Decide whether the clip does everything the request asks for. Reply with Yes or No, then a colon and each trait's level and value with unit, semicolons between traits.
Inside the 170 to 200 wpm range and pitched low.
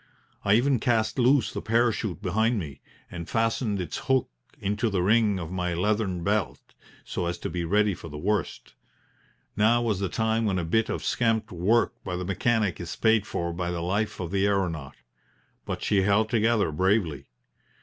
Yes: average, 180 wpm; low, 100 Hz